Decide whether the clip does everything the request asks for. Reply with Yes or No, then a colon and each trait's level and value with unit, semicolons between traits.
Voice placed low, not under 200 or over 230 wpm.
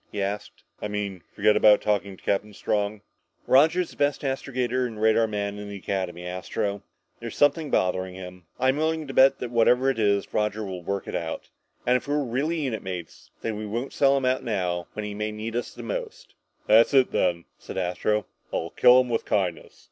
Yes: low, 105 Hz; fast, 205 wpm